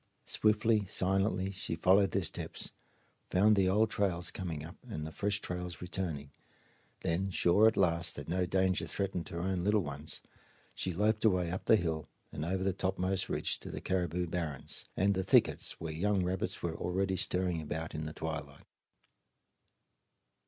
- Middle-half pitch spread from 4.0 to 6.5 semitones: No, average, 2.7 semitones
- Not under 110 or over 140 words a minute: No, average, 165 wpm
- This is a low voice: Yes, very low, 90 Hz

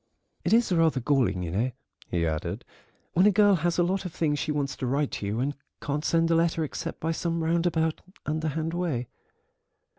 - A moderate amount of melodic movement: Yes, average, 3.7 semitones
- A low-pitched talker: No, medium, 160 Hz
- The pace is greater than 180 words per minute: Yes, average, 200 wpm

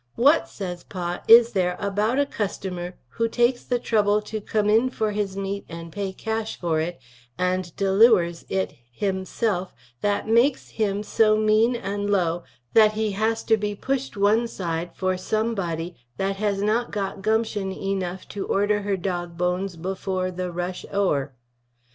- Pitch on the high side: Yes, high, 200 Hz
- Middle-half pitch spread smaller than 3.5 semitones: Yes, average, 3.1 semitones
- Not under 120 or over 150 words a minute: No, average, 165 wpm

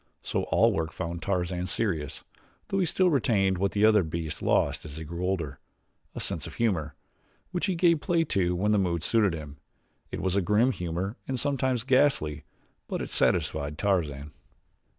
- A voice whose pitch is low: Yes, very low, 95 Hz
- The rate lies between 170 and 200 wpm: Yes, average, 180 wpm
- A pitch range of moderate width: No, wide, 6.1 semitones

